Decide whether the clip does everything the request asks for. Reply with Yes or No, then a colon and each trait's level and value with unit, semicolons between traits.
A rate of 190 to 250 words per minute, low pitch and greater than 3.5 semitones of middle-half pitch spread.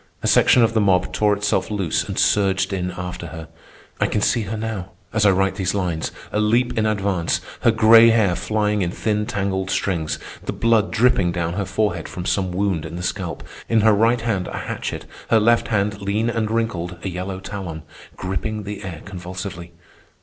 No: average, 195 wpm; low, 100 Hz; average, 3.1 semitones